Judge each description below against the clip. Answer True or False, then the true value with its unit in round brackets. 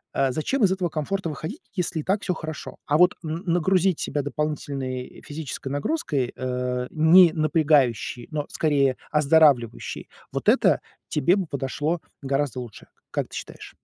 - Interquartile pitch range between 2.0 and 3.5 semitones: False (3.9 semitones)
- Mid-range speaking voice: True (150 Hz)